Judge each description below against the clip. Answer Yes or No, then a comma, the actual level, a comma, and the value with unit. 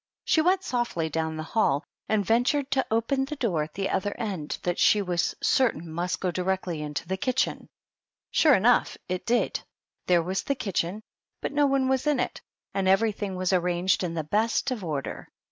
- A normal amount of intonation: No, wide, 6.0 semitones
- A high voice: Yes, high, 195 Hz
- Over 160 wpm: Yes, average, 190 wpm